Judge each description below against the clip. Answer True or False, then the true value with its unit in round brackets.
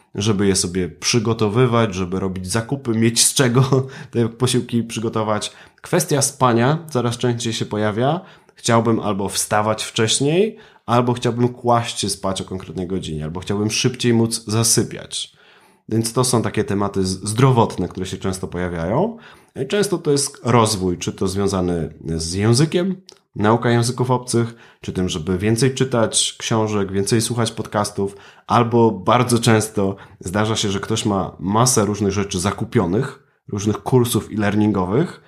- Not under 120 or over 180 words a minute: True (140 wpm)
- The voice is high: False (110 Hz)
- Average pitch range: True (3.5 semitones)